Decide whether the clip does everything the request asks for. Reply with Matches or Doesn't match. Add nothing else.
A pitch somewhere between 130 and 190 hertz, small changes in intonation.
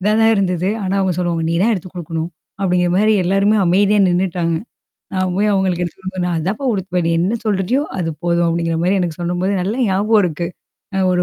Matches